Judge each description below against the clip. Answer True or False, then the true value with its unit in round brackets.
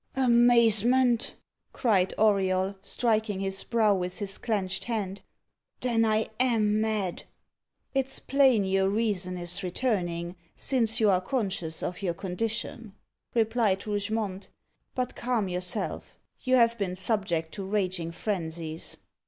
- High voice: True (205 Hz)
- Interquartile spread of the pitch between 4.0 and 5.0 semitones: False (3.6 semitones)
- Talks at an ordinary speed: False (120 wpm)